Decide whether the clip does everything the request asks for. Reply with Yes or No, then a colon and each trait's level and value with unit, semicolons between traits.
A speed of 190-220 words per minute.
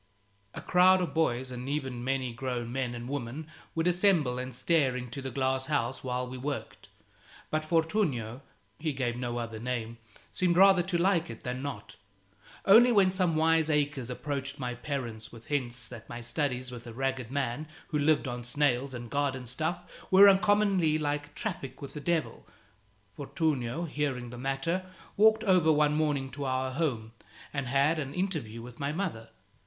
No: average, 170 wpm